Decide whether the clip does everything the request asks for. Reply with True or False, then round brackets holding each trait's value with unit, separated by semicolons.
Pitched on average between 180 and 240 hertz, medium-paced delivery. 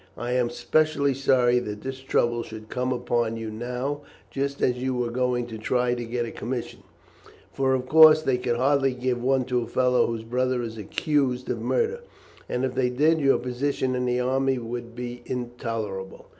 False (125 Hz; 190 wpm)